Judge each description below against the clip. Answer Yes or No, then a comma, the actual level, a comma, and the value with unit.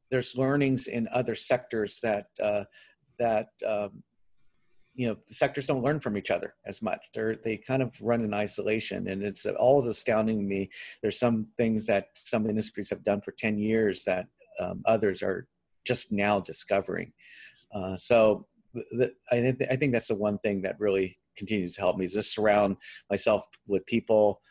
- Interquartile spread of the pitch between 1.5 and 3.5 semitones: Yes, narrow, 2.4 semitones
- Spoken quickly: No, average, 195 wpm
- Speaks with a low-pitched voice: Yes, low, 110 Hz